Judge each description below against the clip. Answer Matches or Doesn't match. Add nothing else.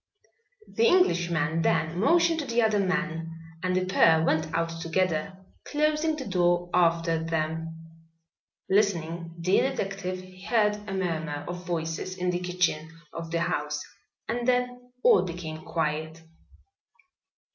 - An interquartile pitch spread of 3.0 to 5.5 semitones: Matches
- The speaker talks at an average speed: Doesn't match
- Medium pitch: Matches